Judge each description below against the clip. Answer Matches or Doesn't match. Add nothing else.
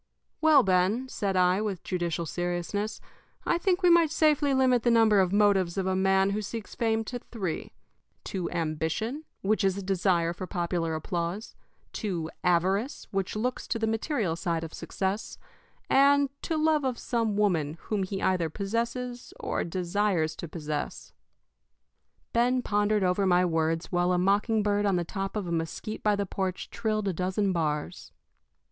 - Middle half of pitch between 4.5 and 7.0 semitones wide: Doesn't match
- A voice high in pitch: Matches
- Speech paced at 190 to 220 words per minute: Doesn't match